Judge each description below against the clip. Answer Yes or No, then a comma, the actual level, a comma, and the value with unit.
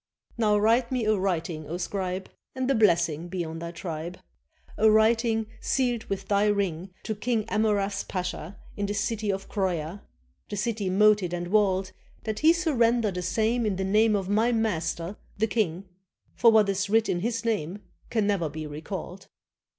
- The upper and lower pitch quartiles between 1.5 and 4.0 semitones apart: Yes, average, 3.4 semitones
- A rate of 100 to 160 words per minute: No, average, 175 wpm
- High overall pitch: Yes, high, 200 Hz